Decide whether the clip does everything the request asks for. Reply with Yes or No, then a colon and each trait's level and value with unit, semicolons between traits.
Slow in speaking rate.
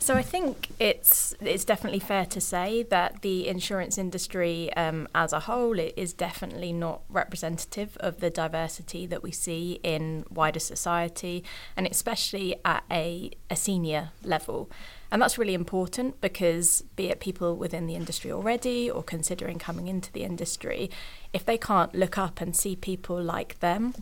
No: average, 165 wpm